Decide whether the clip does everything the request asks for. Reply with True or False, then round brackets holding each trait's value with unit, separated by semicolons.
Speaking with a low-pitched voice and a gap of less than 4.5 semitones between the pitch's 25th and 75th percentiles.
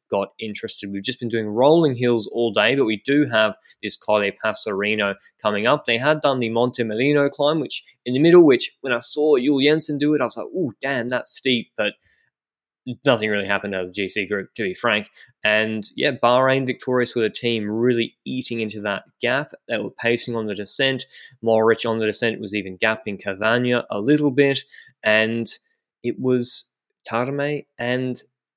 True (120 Hz; 3.9 semitones)